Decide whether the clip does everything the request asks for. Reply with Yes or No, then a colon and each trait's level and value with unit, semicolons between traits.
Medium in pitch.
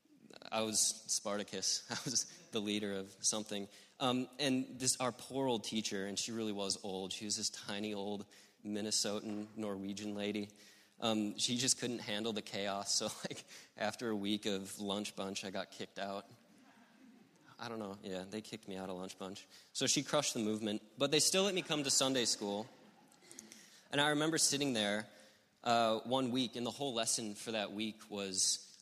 No: low, 110 Hz